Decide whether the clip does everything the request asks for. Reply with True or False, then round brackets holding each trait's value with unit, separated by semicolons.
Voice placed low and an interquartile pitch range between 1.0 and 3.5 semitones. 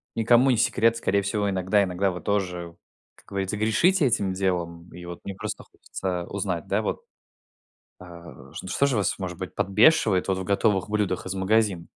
True (95 Hz; 2.9 semitones)